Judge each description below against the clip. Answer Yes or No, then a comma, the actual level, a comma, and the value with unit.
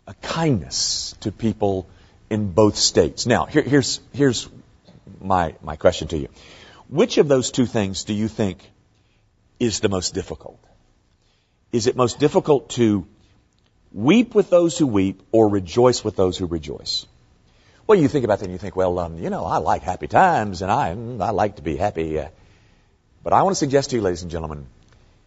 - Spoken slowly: No, average, 185 wpm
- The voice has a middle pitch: No, low, 105 Hz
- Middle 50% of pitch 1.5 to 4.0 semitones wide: No, average, 4.5 semitones